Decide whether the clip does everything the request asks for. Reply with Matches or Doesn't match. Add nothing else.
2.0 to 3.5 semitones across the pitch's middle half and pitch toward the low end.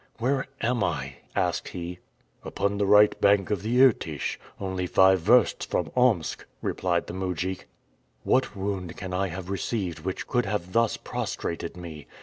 Matches